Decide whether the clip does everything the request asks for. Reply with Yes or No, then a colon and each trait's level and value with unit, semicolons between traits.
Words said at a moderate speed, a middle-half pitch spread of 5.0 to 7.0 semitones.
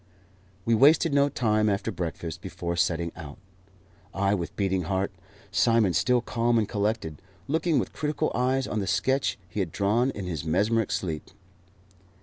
Yes: average, 155 wpm; wide, 5.5 semitones